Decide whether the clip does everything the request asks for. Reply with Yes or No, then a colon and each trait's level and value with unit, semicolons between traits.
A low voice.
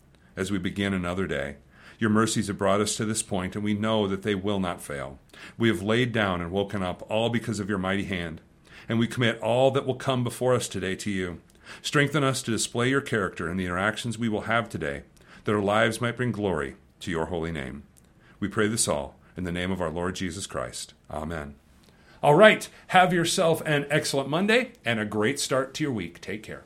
Yes: low, 105 Hz